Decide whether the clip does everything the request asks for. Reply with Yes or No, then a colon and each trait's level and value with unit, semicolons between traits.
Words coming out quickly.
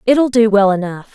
Yes: fast, 210 wpm